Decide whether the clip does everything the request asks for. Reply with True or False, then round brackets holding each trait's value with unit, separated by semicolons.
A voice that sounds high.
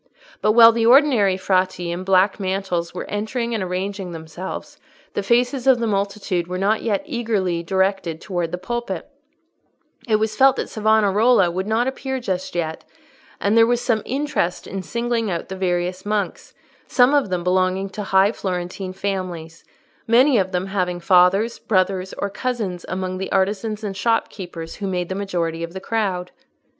True (195 Hz)